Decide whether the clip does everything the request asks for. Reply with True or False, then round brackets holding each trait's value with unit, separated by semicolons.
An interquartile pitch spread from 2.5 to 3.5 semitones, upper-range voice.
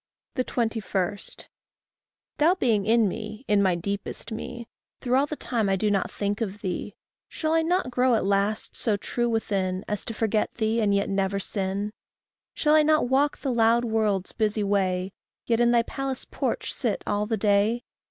True (3.2 semitones; 215 Hz)